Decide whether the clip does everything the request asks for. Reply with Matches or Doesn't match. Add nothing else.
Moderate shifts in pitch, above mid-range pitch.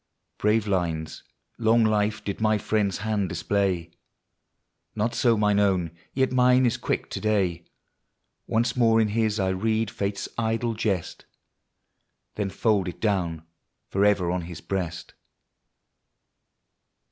Doesn't match